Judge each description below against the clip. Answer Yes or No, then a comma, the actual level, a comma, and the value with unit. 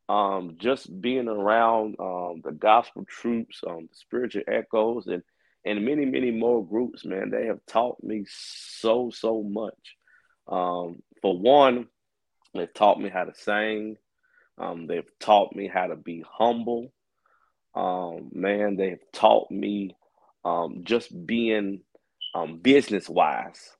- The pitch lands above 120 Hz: No, low, 105 Hz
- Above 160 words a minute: No, average, 140 wpm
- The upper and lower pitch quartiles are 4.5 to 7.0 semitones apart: No, average, 3.7 semitones